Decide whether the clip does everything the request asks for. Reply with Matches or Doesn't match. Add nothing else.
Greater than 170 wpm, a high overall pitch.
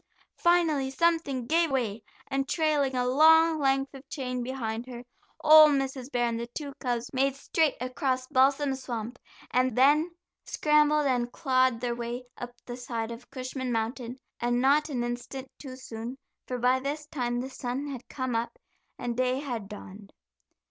Doesn't match